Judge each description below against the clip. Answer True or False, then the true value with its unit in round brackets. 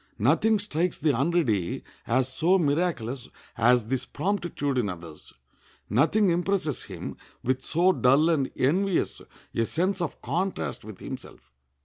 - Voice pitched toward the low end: False (150 Hz)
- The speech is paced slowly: True (130 wpm)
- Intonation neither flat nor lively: False (6.3 semitones)